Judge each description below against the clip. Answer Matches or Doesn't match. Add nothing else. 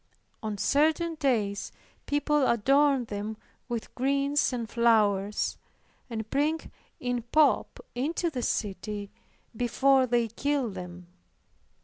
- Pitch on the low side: Doesn't match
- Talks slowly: Matches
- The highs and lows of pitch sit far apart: Doesn't match